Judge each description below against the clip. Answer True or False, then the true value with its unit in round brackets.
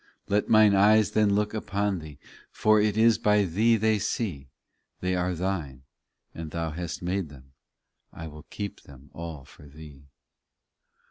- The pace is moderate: True (155 wpm)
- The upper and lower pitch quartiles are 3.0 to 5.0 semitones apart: False (5.4 semitones)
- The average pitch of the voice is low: True (90 Hz)